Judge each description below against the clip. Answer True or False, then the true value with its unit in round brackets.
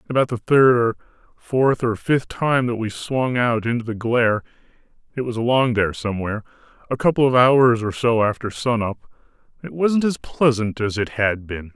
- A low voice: True (120 Hz)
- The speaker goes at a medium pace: True (180 wpm)